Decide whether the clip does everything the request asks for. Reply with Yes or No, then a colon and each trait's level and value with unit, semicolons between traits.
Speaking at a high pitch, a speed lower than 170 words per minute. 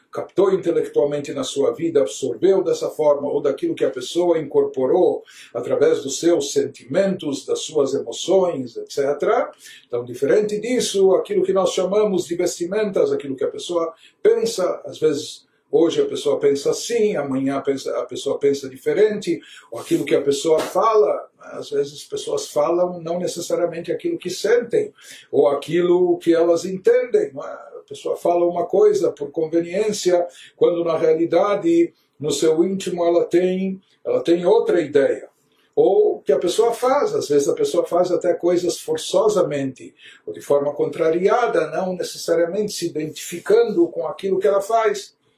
Yes: high, 215 Hz; average, 150 wpm